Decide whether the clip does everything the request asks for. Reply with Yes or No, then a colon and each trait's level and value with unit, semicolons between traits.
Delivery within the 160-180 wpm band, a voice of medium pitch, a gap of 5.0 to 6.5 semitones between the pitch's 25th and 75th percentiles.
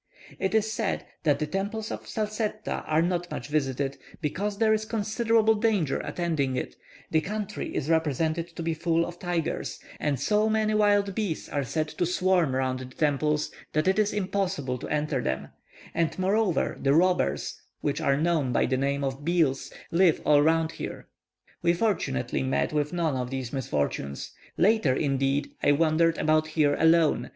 Yes: average, 170 wpm; medium, 160 Hz; wide, 5.5 semitones